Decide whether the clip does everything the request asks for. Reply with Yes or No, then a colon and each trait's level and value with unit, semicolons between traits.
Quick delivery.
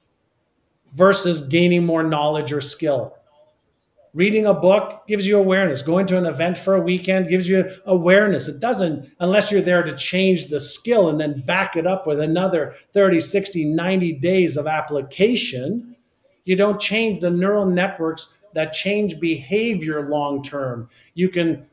No: average, 155 wpm